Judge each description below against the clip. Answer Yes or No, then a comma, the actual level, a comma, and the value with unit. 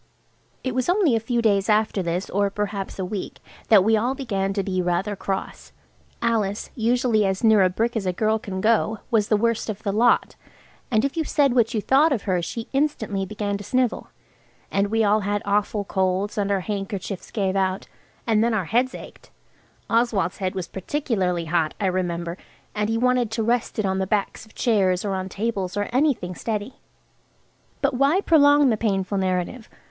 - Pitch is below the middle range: No, high, 210 Hz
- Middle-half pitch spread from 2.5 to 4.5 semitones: Yes, average, 3.4 semitones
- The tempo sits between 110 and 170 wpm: No, average, 195 wpm